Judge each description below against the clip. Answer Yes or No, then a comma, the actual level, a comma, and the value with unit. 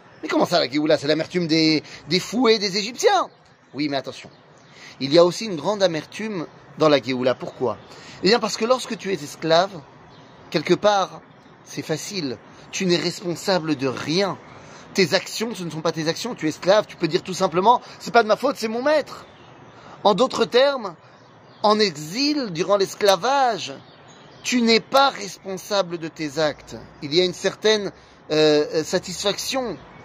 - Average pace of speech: Yes, average, 175 wpm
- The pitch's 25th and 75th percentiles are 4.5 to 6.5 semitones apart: Yes, wide, 5.4 semitones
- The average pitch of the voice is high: No, medium, 180 Hz